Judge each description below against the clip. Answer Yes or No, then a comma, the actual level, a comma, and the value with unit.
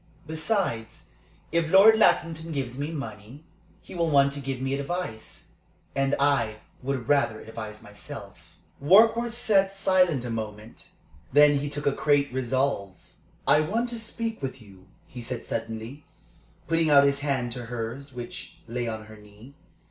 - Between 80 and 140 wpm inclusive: No, average, 155 wpm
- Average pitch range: No, wide, 5.7 semitones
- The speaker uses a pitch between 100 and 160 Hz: Yes, medium, 140 Hz